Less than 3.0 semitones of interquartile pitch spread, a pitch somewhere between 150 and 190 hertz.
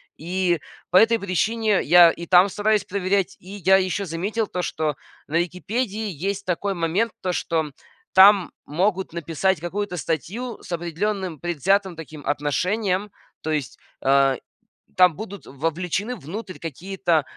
No: average, 3.4 semitones; medium, 185 Hz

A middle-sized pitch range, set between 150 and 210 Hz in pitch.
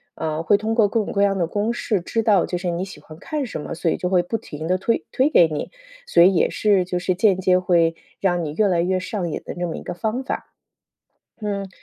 Yes: average, 3.3 semitones; medium, 185 Hz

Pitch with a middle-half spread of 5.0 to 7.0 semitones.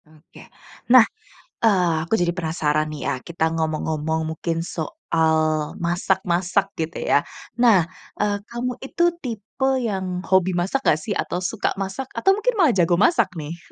Yes: wide, 5.6 semitones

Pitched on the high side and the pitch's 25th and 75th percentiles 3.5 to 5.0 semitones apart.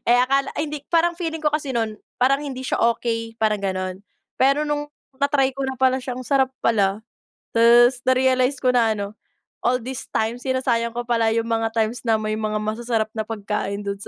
No: high, 240 Hz; average, 3.1 semitones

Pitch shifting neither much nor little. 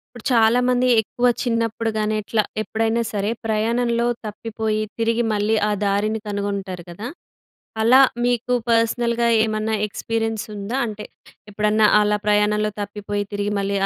No: narrow, 1.7 semitones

